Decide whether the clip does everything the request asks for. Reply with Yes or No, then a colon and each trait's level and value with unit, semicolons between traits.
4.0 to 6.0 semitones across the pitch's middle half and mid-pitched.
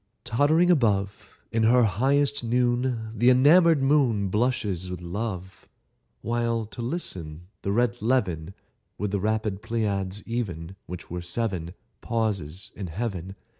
No: average, 4.3 semitones; low, 110 Hz